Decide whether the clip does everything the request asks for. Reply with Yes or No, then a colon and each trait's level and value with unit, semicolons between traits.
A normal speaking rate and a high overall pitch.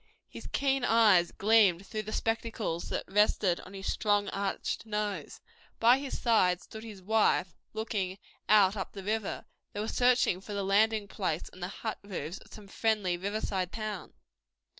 Yes: average, 170 wpm; high, 205 Hz